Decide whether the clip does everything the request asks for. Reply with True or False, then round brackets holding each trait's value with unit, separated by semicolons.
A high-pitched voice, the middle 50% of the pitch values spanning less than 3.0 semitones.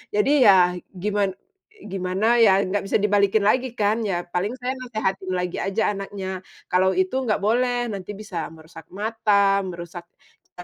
True (200 Hz; 2.6 semitones)